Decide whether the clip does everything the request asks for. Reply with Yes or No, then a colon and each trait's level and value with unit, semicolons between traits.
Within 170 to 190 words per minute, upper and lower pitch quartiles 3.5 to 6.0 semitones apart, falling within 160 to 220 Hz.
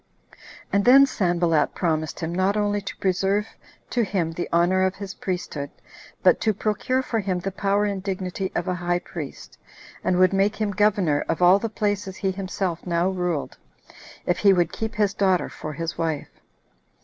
No: average, 180 wpm; average, 2.7 semitones; high, 190 Hz